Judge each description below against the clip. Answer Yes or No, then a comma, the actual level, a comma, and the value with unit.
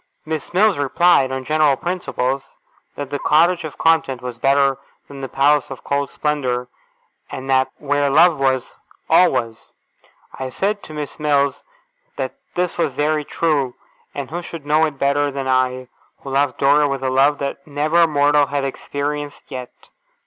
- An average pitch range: No, narrow, 2.3 semitones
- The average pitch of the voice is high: No, medium, 145 Hz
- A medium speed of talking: Yes, average, 165 wpm